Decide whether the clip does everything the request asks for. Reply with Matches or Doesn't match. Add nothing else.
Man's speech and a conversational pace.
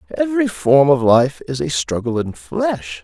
Matches